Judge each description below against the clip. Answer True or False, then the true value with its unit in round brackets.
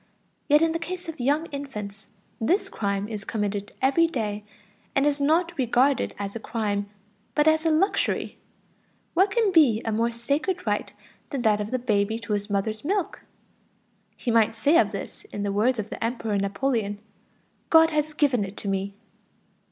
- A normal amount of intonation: False (6.9 semitones)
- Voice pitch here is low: False (235 Hz)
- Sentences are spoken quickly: False (175 wpm)